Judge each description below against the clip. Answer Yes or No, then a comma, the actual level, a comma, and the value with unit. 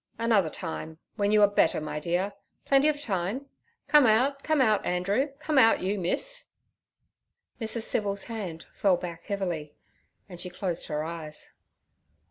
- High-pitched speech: Yes, high, 200 Hz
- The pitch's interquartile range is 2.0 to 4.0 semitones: No, average, 5.1 semitones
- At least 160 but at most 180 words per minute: No, average, 145 wpm